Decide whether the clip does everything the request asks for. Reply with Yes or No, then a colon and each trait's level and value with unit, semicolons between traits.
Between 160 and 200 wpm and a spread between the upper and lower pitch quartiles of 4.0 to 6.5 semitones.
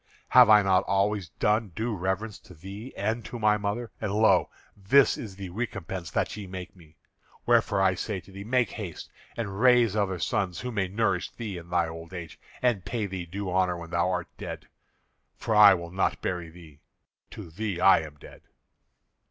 No: average, 195 wpm; average, 3.3 semitones